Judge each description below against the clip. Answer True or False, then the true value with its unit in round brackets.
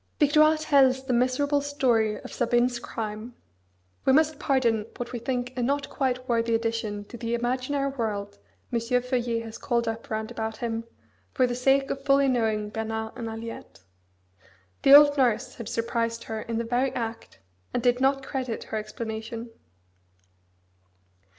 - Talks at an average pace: True (155 wpm)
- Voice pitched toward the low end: False (240 Hz)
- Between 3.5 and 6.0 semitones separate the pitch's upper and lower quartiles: False (2.8 semitones)